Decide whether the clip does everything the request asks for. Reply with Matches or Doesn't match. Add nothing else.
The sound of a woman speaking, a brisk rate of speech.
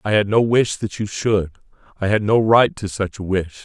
Doesn't match